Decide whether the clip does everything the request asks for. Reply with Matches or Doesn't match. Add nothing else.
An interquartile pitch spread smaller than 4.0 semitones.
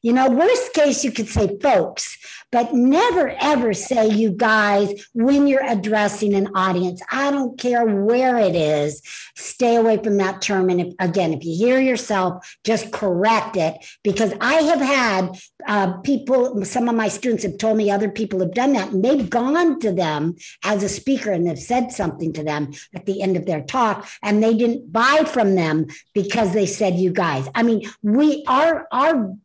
Doesn't match